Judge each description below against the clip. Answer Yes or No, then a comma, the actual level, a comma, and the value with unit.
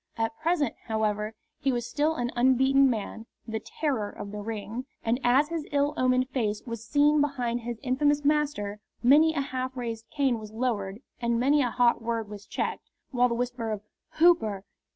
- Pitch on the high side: Yes, high, 245 Hz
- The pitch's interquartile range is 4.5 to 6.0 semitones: No, average, 3.9 semitones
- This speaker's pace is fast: No, average, 180 wpm